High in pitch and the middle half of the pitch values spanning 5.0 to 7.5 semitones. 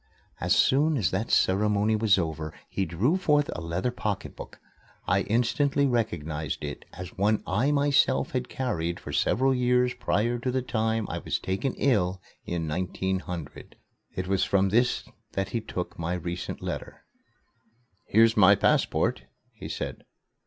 No: low, 105 Hz; wide, 5.4 semitones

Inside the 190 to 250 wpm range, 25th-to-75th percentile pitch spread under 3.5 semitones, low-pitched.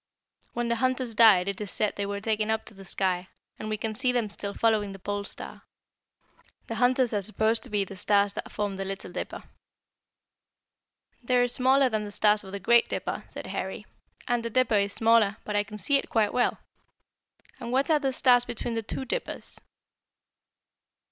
No: average, 200 wpm; average, 3.1 semitones; high, 220 Hz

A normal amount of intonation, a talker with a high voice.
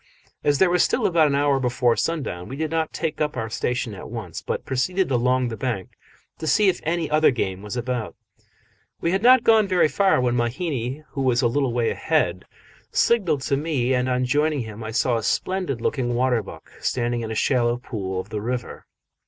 No: average, 4.7 semitones; low, 130 Hz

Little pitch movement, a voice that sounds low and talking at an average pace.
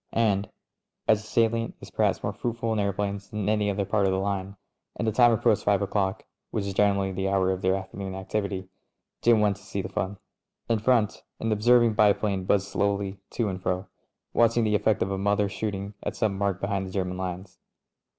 No: narrow, 2.0 semitones; low, 100 Hz; fast, 210 wpm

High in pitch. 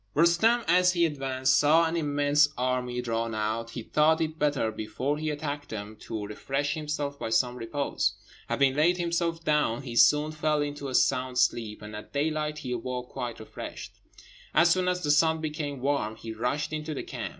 No: medium, 145 Hz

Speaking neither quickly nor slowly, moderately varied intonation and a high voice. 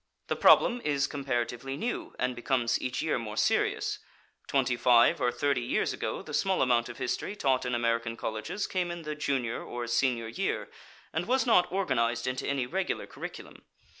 No: average, 175 wpm; average, 4.2 semitones; low, 130 Hz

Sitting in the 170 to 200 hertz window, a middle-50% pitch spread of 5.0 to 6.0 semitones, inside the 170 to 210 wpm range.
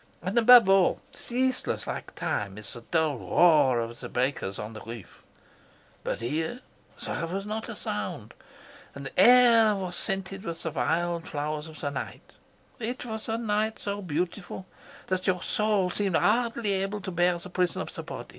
Yes: medium, 185 Hz; average, 5.3 semitones; average, 175 wpm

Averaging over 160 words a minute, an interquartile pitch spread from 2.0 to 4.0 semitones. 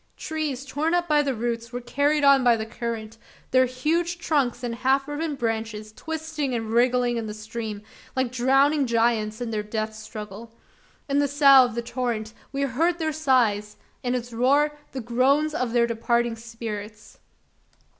Yes: average, 170 wpm; average, 3.7 semitones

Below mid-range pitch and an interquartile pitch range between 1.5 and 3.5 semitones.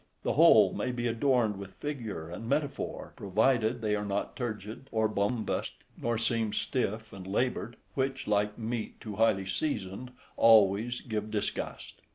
Yes: low, 110 Hz; average, 2.9 semitones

